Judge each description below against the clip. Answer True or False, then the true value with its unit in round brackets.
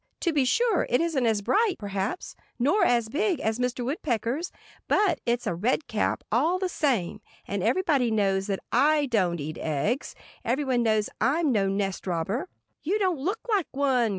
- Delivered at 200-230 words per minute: False (175 wpm)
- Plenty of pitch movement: True (7.4 semitones)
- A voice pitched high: True (250 Hz)